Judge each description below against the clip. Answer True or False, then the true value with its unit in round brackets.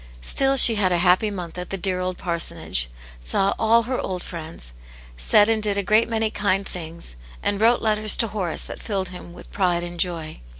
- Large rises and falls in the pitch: False (3.7 semitones)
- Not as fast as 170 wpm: False (205 wpm)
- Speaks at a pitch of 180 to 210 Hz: True (190 Hz)